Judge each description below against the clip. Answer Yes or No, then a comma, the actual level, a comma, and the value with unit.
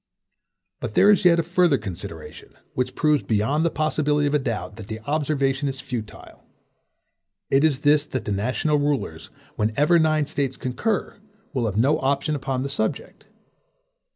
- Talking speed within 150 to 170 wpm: Yes, average, 160 wpm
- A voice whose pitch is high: No, medium, 140 Hz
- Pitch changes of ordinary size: Yes, average, 4.0 semitones